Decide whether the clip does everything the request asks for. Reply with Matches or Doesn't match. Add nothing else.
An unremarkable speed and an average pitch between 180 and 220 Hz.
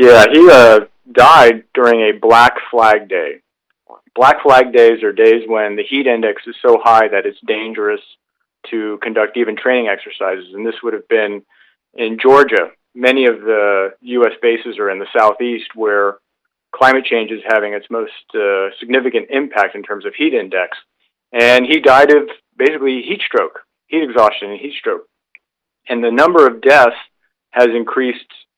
Doesn't match